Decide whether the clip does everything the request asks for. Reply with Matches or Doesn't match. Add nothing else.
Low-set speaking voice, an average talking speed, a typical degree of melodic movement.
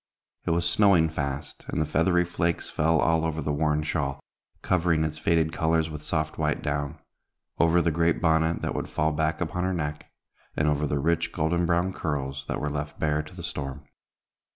Doesn't match